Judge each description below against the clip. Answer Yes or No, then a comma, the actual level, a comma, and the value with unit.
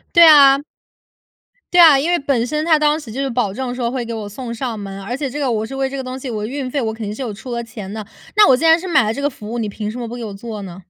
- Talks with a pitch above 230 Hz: Yes, high, 245 Hz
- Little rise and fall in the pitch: No, average, 4.0 semitones